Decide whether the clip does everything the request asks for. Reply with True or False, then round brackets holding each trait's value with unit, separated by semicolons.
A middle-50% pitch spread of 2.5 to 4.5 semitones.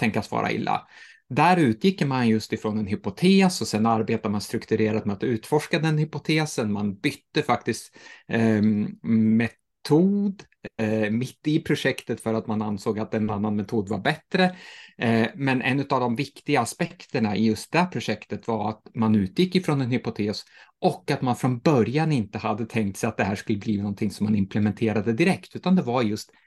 False (5.5 semitones)